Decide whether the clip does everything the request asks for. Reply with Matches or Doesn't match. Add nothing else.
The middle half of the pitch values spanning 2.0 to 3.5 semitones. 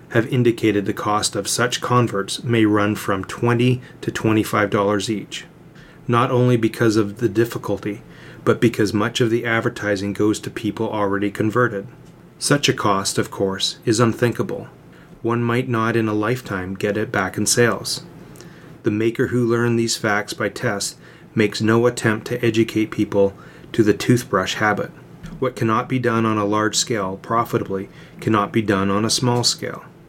Matches